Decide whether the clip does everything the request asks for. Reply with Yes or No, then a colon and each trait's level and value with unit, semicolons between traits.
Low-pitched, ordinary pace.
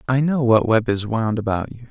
No: low, 115 Hz; fast, 250 wpm